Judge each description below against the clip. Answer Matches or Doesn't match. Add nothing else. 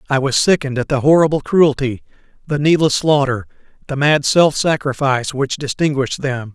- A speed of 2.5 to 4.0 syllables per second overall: Doesn't match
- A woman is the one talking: Doesn't match